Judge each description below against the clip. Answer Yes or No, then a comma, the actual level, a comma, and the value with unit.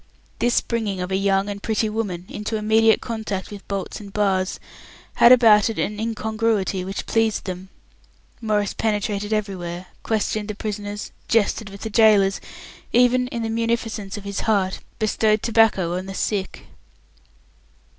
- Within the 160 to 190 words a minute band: No, average, 150 wpm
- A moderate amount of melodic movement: No, narrow, 2.2 semitones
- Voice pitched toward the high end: Yes, high, 210 Hz